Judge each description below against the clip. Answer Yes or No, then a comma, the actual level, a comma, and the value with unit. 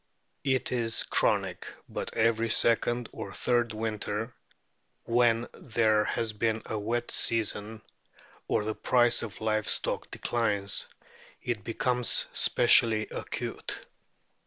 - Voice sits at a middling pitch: No, low, 115 Hz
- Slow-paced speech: Yes, slow, 110 wpm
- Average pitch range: No, narrow, 1.7 semitones